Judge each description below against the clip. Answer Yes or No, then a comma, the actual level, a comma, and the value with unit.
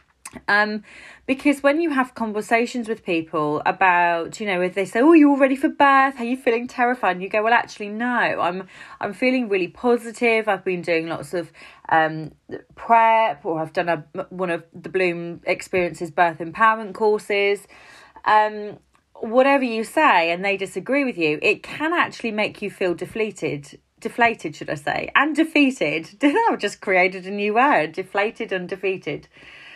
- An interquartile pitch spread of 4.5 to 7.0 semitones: Yes, average, 4.9 semitones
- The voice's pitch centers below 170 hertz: No, high, 205 Hz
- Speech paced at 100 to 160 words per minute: No, average, 170 wpm